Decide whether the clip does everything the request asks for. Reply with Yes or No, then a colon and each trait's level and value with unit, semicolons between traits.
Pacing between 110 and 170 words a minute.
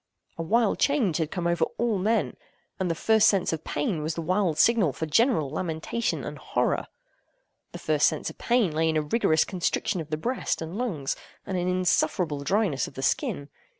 No: average, 195 wpm